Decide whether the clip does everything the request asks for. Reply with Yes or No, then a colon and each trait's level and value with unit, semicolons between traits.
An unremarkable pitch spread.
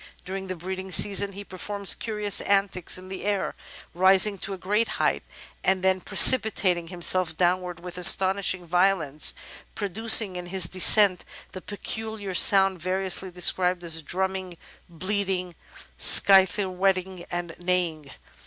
No: narrow, 1.6 semitones